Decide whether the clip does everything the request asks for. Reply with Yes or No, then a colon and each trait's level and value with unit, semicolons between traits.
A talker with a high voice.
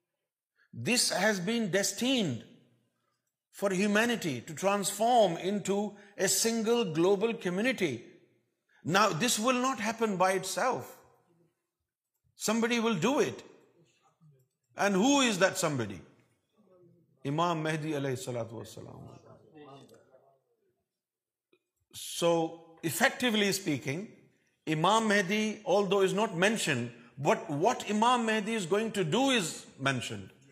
Yes: high, 195 Hz